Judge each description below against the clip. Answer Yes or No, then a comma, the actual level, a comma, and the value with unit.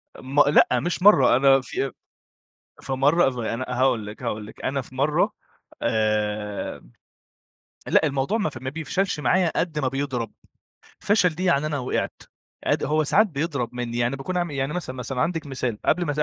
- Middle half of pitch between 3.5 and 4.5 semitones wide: Yes, average, 4.2 semitones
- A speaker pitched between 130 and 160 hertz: Yes, low, 135 Hz